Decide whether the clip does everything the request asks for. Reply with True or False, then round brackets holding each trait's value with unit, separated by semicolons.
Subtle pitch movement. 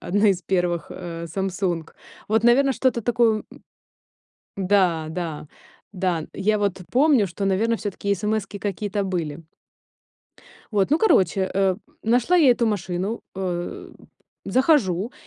False (3.8 semitones)